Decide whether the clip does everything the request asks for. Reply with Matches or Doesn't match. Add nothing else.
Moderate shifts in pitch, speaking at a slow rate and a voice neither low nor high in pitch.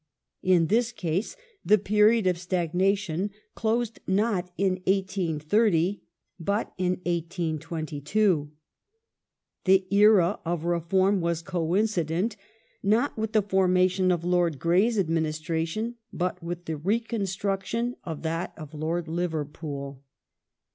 Matches